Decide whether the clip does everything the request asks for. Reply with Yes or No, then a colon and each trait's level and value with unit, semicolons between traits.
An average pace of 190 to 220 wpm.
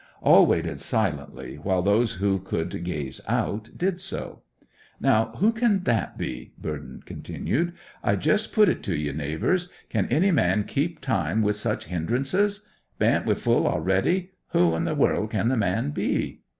No: average, 165 wpm